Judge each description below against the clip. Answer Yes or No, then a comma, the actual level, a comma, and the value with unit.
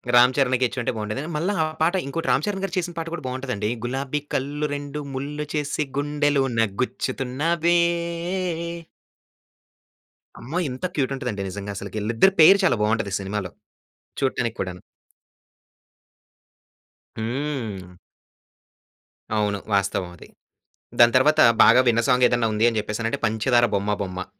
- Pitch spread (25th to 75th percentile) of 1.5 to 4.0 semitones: No, wide, 5.5 semitones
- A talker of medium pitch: No, low, 125 Hz